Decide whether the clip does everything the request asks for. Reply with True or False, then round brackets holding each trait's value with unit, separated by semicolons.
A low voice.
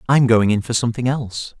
True (115 Hz)